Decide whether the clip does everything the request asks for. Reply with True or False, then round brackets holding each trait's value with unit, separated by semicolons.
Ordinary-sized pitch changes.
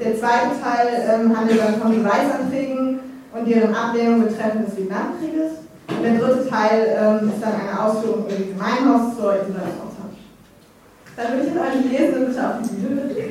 True (3.1 semitones)